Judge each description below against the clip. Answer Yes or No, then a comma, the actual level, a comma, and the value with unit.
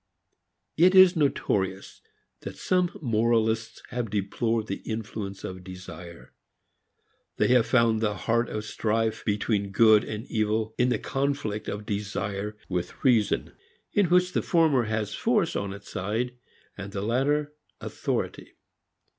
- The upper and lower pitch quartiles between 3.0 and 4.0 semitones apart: Yes, average, 3.4 semitones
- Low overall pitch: Yes, low, 110 Hz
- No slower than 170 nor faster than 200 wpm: No, slow, 135 wpm